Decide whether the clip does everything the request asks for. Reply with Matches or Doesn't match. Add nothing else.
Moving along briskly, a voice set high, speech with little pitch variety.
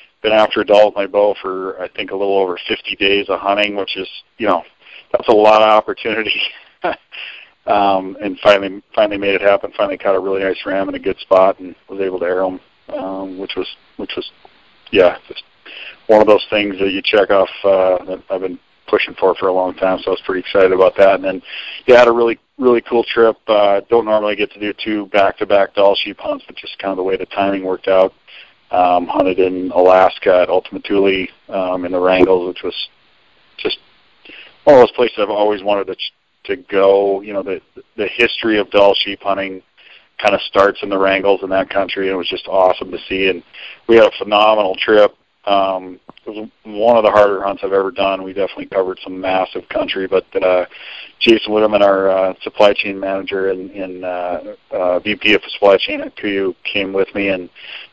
Doesn't match